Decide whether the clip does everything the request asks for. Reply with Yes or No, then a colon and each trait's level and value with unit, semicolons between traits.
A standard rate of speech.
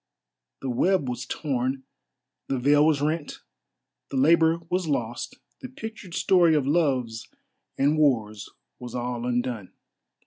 No: slow, 130 wpm